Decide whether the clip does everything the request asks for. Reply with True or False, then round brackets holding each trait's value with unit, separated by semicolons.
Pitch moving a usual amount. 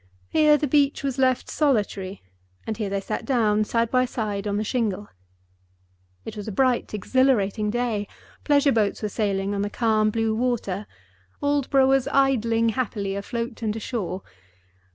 True (3.9 semitones)